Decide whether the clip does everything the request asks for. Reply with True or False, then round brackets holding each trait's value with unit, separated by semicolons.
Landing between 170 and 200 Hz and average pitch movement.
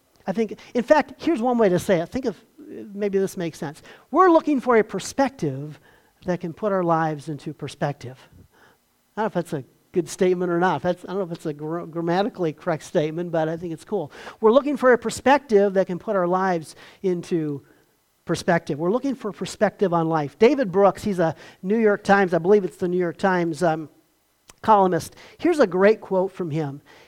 True (185 Hz; 4.4 semitones)